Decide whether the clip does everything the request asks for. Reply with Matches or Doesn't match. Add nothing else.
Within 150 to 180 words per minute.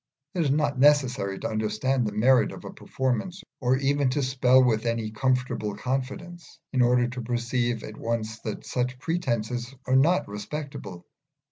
Matches